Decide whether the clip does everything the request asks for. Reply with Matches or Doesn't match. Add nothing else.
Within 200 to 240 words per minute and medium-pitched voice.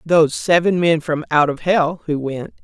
Matches